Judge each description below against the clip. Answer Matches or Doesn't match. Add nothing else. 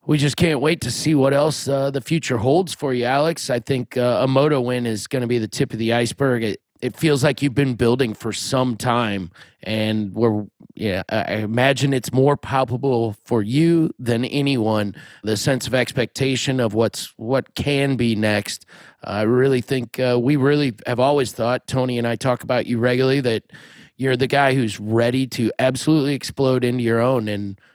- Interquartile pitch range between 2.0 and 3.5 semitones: Matches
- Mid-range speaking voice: Doesn't match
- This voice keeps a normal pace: Matches